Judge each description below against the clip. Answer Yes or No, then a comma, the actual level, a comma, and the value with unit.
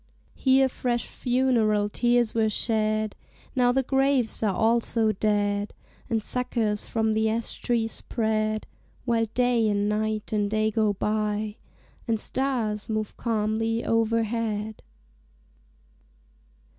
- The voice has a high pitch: Yes, high, 220 Hz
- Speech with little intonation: Yes, narrow, 1.8 semitones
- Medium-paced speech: No, slow, 115 wpm